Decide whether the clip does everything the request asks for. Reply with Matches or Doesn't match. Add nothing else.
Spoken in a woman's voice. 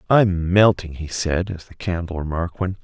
Doesn't match